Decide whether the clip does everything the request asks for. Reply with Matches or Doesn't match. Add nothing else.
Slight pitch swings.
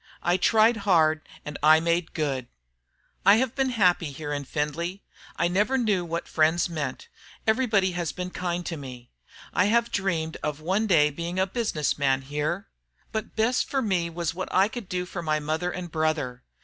Doesn't match